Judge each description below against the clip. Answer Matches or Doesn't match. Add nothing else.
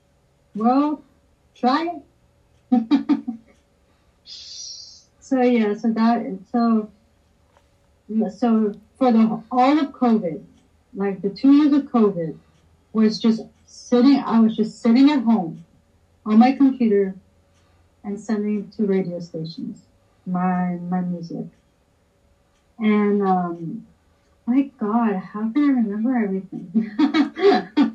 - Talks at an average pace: Doesn't match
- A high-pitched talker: Matches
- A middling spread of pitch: Doesn't match